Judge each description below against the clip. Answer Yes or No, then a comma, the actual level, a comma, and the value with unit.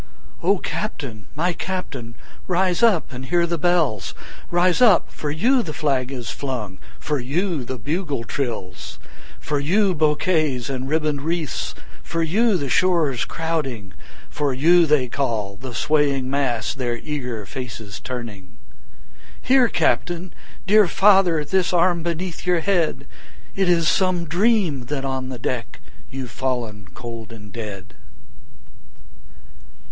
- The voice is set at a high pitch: No, medium, 150 Hz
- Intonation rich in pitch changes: Yes, wide, 6.0 semitones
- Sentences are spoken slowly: Yes, slow, 130 wpm